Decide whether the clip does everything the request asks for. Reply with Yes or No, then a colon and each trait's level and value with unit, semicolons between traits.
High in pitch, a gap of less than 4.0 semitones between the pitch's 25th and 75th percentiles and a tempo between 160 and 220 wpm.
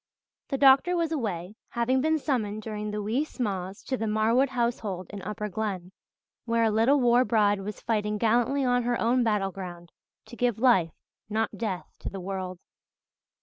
Yes: high, 220 Hz; average, 3.5 semitones; average, 170 wpm